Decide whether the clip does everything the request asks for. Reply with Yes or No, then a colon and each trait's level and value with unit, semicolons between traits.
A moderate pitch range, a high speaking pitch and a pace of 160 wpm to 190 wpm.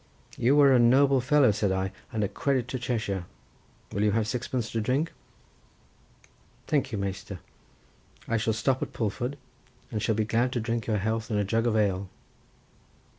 No: average, 3.4 semitones; low, 115 Hz; average, 175 wpm